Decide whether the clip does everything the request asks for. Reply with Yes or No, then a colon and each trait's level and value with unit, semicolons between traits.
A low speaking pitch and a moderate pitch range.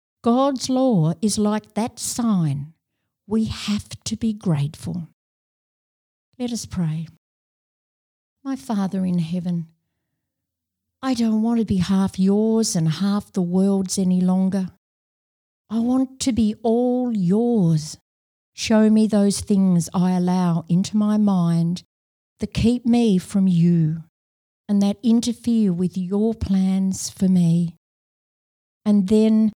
No: high, 195 Hz; average, 4.2 semitones